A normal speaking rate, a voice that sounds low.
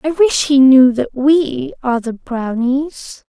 No: average, 165 wpm; very high, 275 Hz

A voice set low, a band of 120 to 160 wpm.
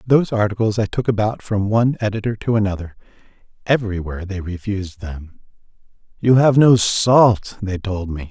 Yes: low, 105 Hz; average, 150 wpm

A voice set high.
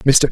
No: medium, 150 Hz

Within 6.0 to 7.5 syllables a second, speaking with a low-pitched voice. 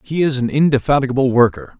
Yes: 6.5 syllables/s; low, 130 Hz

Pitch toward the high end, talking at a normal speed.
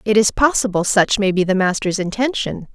Yes: high, 205 Hz; average, 195 wpm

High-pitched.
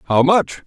No: medium, 160 Hz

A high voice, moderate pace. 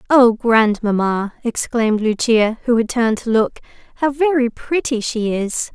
Yes: high, 235 Hz; average, 145 wpm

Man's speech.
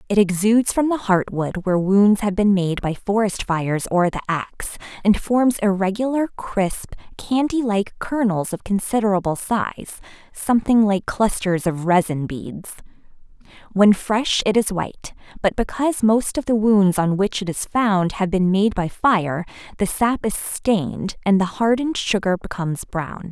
No: female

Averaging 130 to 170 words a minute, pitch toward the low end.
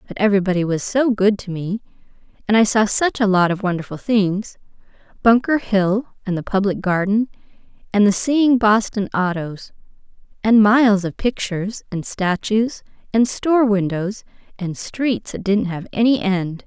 No: average, 150 wpm; high, 205 Hz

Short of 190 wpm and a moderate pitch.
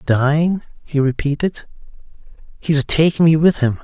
Yes: average, 140 wpm; medium, 150 Hz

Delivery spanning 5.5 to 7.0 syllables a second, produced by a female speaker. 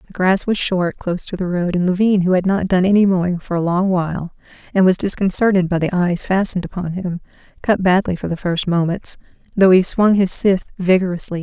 Yes: 5.8 syllables/s; female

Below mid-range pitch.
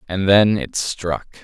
Yes: very low, 95 Hz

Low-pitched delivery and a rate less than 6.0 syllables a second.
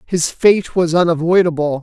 No: medium, 170 Hz; 4.7 syllables/s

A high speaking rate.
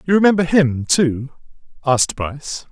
No: slow, 135 wpm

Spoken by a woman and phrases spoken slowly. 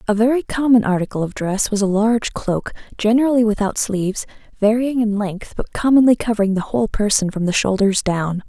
No: female; average, 185 wpm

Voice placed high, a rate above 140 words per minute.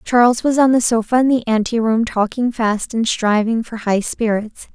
Yes: high, 230 Hz; average, 200 wpm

